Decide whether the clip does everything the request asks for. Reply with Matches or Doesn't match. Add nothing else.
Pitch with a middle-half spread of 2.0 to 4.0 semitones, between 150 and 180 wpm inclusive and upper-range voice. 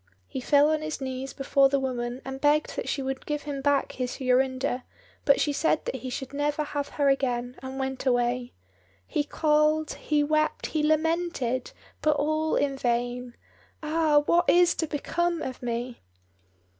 Matches